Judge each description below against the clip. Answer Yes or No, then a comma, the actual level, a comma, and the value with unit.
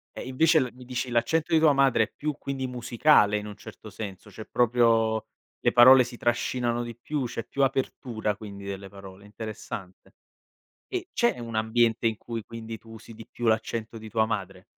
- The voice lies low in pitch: Yes, low, 115 Hz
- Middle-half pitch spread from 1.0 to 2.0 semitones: No, narrow, 2.6 semitones